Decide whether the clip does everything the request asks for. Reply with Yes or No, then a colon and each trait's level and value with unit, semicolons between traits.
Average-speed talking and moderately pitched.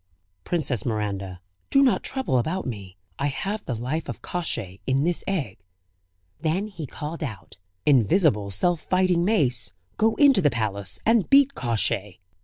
Yes: average, 150 wpm; medium, 145 Hz